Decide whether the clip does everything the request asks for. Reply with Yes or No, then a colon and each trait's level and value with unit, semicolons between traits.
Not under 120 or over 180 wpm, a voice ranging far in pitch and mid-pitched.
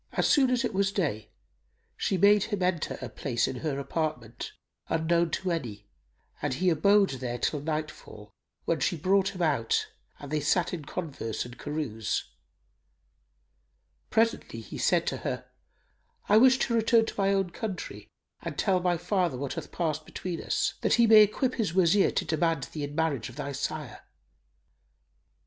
Yes: average, 170 wpm; wide, 5.7 semitones; medium, 165 Hz